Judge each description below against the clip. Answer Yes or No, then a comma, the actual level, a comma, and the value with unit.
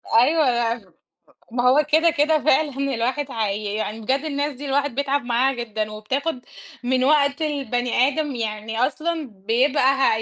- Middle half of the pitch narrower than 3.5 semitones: No, average, 4.0 semitones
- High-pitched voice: Yes, very high, 260 Hz